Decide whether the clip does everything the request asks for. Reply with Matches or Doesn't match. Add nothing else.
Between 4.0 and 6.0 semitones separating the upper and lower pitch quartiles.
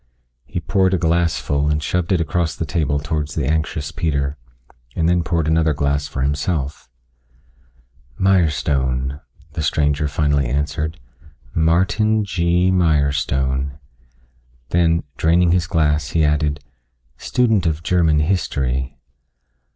Doesn't match